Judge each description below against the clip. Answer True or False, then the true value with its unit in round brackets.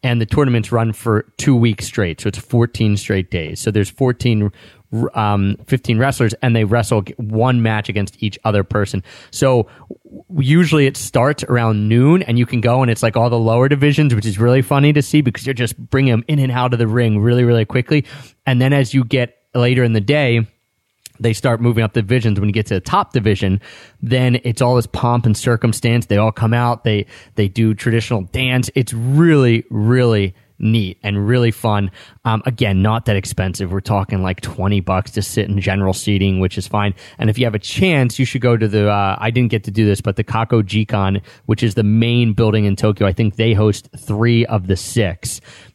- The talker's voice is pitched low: True (115 Hz)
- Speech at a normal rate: False (215 wpm)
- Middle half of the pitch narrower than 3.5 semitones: True (2.8 semitones)